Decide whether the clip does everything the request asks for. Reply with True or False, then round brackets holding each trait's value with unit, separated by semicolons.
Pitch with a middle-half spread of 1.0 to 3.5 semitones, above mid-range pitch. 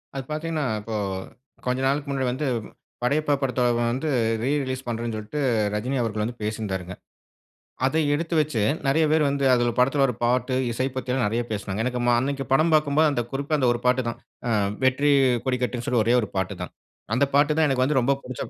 False (3.1 semitones; 130 Hz)